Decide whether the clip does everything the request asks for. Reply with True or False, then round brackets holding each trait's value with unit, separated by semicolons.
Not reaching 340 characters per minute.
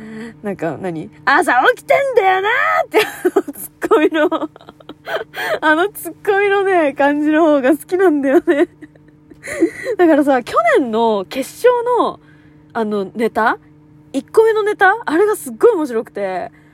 True (280 characters per minute)